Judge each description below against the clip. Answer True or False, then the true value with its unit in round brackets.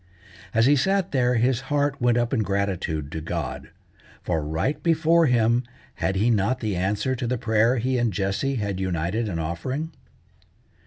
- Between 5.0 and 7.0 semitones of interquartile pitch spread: True (5.3 semitones)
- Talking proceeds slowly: False (170 wpm)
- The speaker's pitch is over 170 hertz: False (115 Hz)